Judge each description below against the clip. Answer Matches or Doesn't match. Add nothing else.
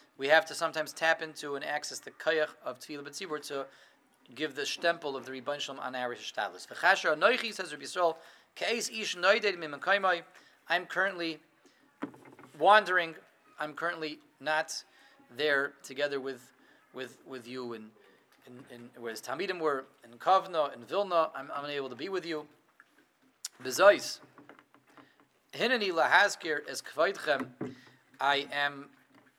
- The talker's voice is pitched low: Doesn't match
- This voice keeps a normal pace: Doesn't match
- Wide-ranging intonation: Doesn't match